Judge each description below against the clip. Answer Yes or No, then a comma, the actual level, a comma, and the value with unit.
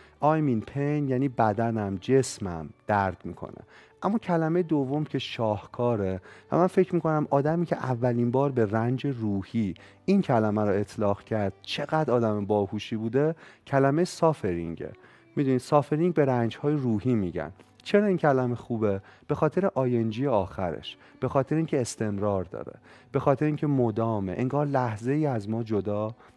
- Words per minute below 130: No, average, 150 wpm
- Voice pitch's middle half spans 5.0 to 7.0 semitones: Yes, wide, 5.6 semitones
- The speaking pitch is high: No, low, 125 Hz